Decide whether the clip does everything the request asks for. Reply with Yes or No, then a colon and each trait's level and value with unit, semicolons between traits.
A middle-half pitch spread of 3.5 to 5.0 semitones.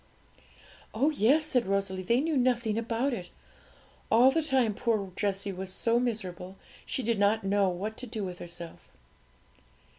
Yes: average, 4.2 semitones